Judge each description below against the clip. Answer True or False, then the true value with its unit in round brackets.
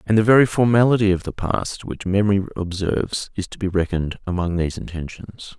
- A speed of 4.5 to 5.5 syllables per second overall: False (5.9 syllables/s)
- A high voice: False (95 Hz)